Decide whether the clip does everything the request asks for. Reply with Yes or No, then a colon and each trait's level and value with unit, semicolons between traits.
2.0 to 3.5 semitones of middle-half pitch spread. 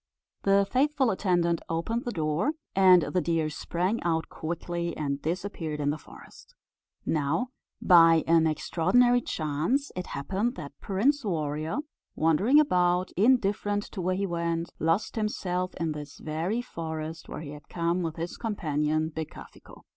No: average, 4.0 semitones